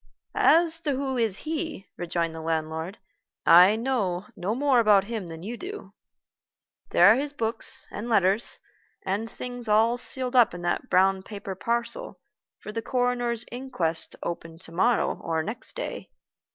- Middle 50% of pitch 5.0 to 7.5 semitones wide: Yes, wide, 5.5 semitones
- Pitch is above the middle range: Yes, high, 220 Hz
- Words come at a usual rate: Yes, average, 160 wpm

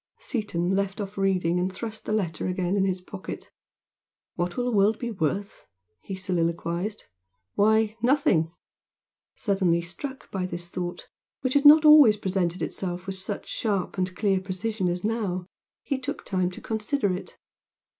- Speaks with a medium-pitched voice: No, high, 195 Hz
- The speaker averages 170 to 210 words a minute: No, average, 155 wpm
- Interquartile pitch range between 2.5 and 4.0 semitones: Yes, average, 3.3 semitones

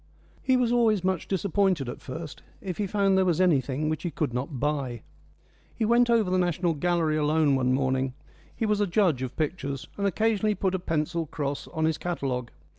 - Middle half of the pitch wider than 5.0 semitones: Yes, wide, 5.6 semitones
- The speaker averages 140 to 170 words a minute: No, average, 200 wpm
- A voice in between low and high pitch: Yes, medium, 170 Hz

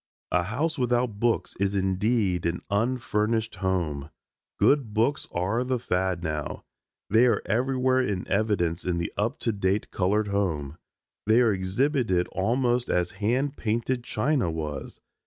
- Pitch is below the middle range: Yes, low, 105 Hz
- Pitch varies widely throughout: No, average, 5.0 semitones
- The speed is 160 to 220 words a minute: No, average, 140 wpm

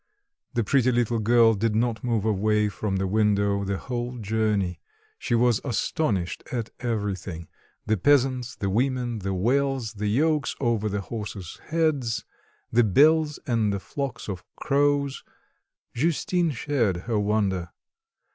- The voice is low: Yes, low, 115 Hz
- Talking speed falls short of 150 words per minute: Yes, slow, 135 wpm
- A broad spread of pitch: No, average, 4.1 semitones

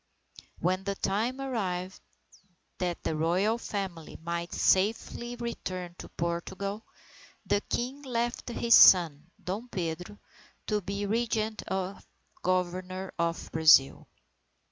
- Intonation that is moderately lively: Yes, average, 4.1 semitones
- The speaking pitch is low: No, high, 190 Hz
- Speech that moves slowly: Yes, slow, 110 wpm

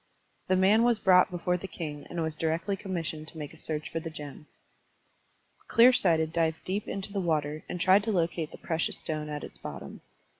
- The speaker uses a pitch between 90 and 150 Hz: No, medium, 165 Hz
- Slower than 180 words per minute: No, average, 200 wpm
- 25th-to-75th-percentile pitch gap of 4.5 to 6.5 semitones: No, average, 3.3 semitones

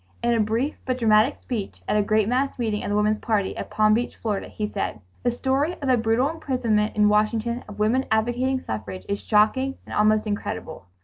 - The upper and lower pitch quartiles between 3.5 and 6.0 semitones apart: No, average, 3.0 semitones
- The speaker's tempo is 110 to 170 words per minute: No, fast, 205 wpm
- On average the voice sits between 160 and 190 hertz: No, high, 220 Hz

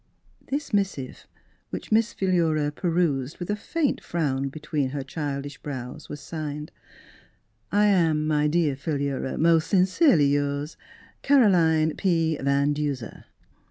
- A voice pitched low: No, medium, 155 Hz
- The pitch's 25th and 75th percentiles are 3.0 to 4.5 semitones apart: Yes, average, 3.7 semitones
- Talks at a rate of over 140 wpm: No, slow, 135 wpm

